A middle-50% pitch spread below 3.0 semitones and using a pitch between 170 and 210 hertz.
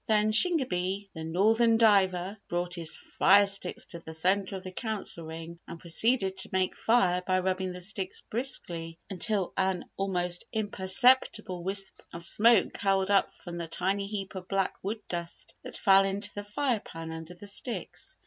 Yes: narrow, 2.6 semitones; high, 190 Hz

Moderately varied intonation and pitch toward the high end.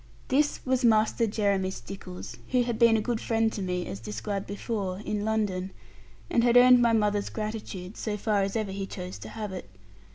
Yes: average, 3.0 semitones; high, 210 Hz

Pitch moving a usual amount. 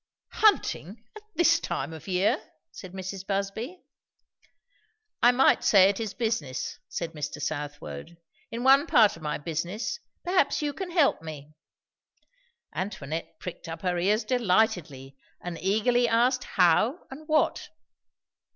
No: wide, 7.1 semitones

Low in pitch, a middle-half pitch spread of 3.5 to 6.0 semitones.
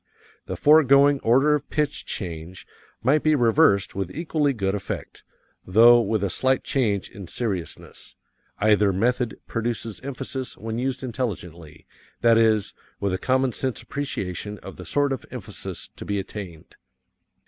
Yes: low, 115 Hz; average, 5.2 semitones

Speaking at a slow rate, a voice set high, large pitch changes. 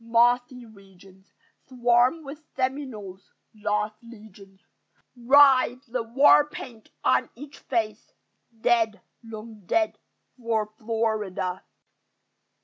No: slow, 90 wpm; high, 230 Hz; average, 3.3 semitones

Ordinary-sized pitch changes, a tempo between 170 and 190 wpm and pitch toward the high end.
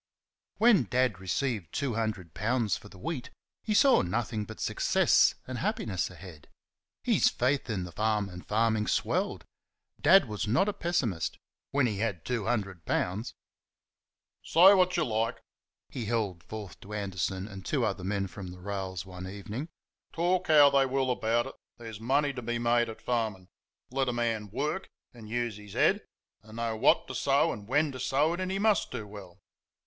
No: average, 5.0 semitones; average, 180 wpm; low, 115 Hz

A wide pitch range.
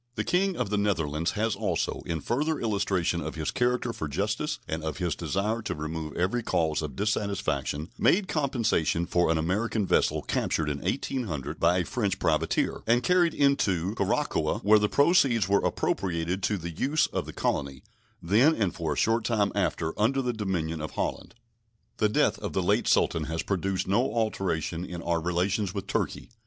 Yes: wide, 5.9 semitones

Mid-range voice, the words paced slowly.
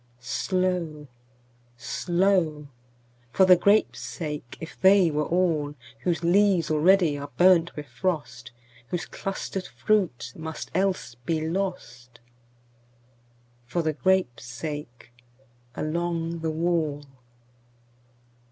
Yes: medium, 155 Hz; slow, 90 wpm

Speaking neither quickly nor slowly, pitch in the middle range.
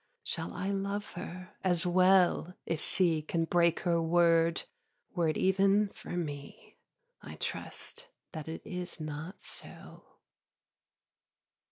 No: slow, 125 wpm; medium, 175 Hz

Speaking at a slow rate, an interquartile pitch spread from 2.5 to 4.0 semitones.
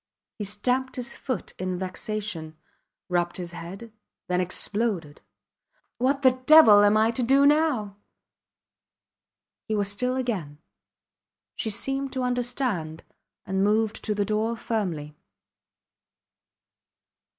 No: slow, 115 wpm; average, 5.2 semitones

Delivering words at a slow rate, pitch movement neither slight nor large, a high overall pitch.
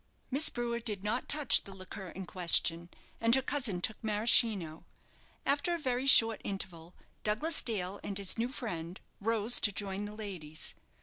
No: average, 165 wpm; average, 4.3 semitones; high, 210 Hz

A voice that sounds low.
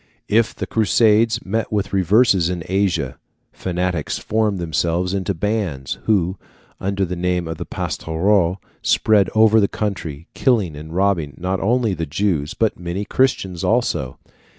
Yes: very low, 95 Hz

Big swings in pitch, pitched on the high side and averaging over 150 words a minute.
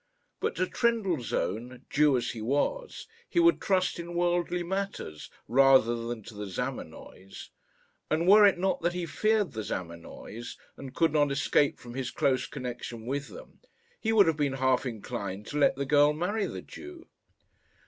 No: wide, 6.9 semitones; medium, 145 Hz; average, 170 wpm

